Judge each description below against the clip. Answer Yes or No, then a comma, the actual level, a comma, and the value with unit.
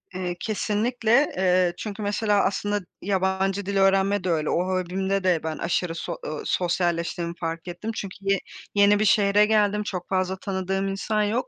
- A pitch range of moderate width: No, narrow, 2.2 semitones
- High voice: Yes, high, 195 Hz